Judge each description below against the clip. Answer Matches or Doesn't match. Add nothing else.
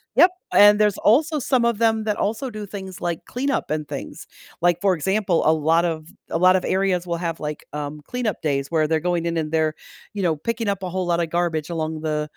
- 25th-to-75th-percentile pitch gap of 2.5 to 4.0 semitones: Doesn't match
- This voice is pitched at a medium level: Matches